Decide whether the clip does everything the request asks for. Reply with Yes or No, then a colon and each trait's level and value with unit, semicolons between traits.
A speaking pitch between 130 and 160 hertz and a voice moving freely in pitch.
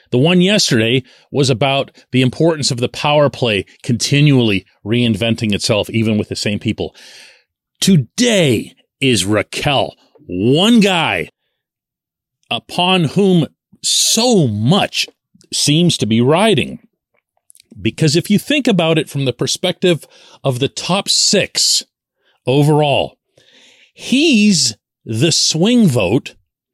Yes: medium, 140 Hz; wide, 6.8 semitones